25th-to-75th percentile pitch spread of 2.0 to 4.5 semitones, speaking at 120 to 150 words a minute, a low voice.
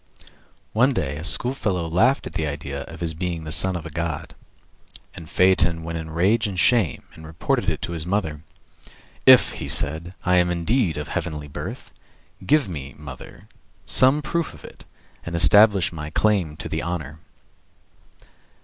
No: average, 3.7 semitones; average, 165 wpm; very low, 85 Hz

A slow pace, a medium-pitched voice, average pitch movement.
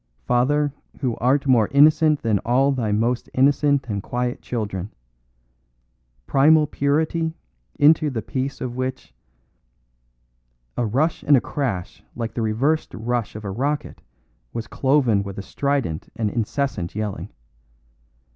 No: slow, 130 wpm; low, 125 Hz; average, 4.6 semitones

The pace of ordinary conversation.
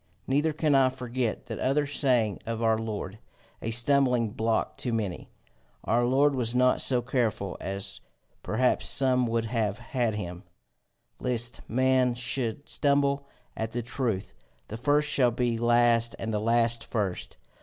Yes: average, 150 wpm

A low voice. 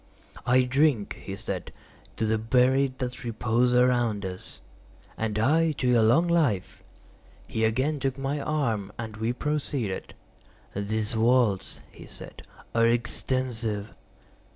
Yes: low, 120 Hz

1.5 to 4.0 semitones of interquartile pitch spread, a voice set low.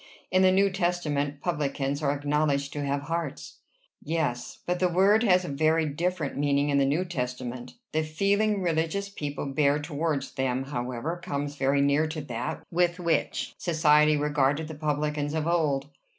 No: average, 3.2 semitones; medium, 150 Hz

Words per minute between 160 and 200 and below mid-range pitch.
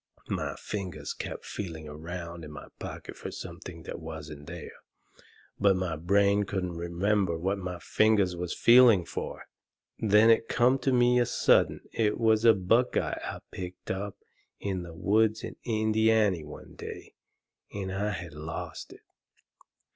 No: average, 145 wpm; very low, 95 Hz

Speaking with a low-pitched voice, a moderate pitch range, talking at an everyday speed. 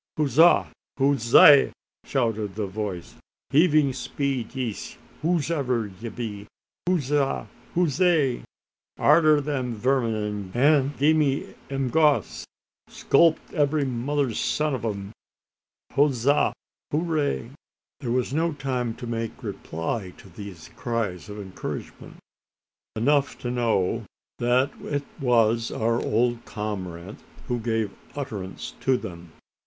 No: low, 125 Hz; average, 4.8 semitones; slow, 110 wpm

